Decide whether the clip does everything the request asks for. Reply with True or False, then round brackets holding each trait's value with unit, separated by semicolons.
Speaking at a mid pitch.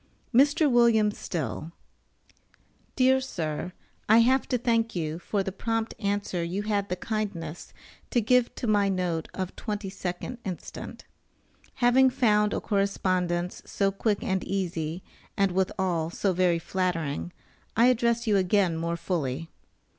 False (195 Hz)